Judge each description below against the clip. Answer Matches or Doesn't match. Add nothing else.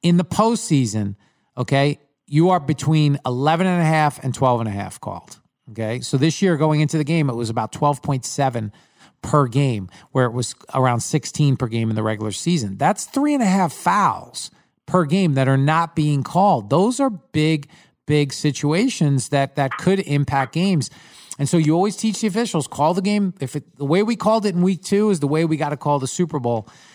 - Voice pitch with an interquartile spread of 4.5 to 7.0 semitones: Matches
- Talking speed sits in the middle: Doesn't match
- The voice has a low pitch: Doesn't match